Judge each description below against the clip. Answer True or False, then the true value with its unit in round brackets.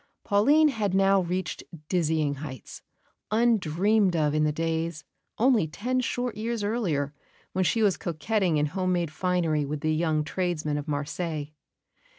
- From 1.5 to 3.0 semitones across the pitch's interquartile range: False (5.2 semitones)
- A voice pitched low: False (175 Hz)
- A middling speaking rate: True (150 wpm)